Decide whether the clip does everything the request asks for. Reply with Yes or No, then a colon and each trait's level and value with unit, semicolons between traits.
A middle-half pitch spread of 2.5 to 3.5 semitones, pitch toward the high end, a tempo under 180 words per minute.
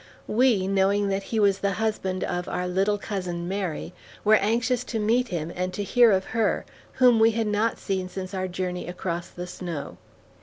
No: average, 3.2 semitones; high, 195 Hz; average, 190 wpm